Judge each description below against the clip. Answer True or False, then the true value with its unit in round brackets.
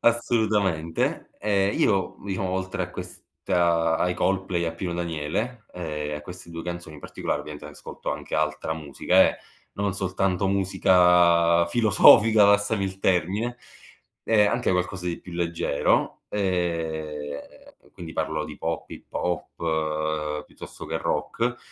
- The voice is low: True (90 Hz)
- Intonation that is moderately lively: True (3.2 semitones)